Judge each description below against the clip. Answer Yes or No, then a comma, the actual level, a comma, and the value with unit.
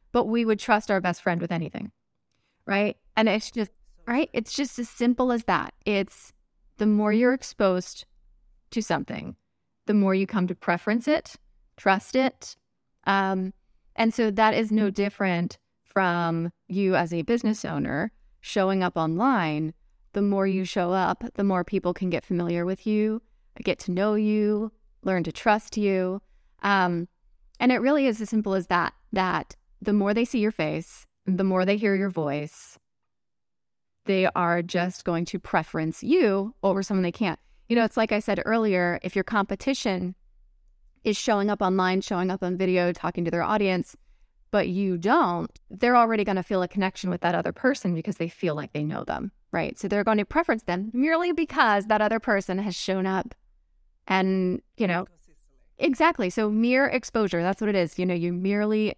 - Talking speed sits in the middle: Yes, average, 180 wpm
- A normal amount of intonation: Yes, average, 3.2 semitones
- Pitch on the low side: No, high, 195 Hz